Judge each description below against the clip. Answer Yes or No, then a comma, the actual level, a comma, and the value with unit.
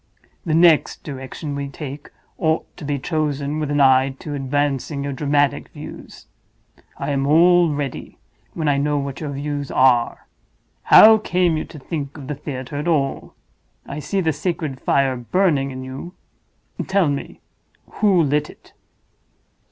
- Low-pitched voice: No, medium, 145 Hz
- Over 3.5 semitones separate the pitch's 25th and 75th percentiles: No, narrow, 2.5 semitones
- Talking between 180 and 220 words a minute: No, average, 155 wpm